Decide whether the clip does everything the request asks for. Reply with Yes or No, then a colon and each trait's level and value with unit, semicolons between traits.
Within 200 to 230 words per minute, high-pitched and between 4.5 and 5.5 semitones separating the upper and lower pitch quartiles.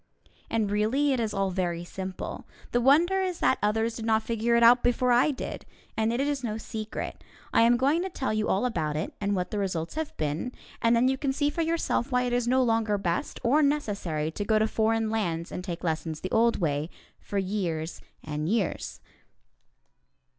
Yes: fast, 205 wpm; high, 220 Hz; average, 5.0 semitones